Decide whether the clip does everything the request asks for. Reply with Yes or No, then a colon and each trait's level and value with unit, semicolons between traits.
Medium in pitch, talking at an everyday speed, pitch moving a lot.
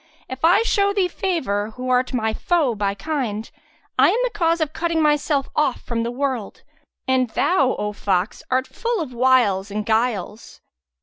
No: very high, 255 Hz; average, 175 wpm; wide, 6.6 semitones